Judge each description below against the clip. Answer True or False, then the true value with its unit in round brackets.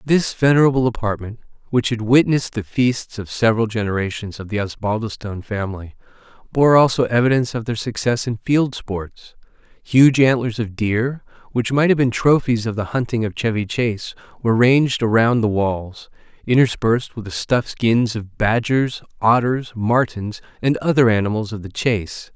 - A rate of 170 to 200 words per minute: False (160 wpm)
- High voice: False (115 Hz)